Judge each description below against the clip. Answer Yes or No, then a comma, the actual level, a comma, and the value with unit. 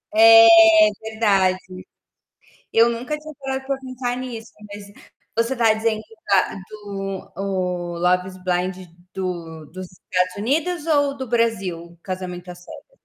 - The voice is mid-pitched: No, high, 205 Hz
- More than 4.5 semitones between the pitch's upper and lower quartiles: Yes, average, 4.9 semitones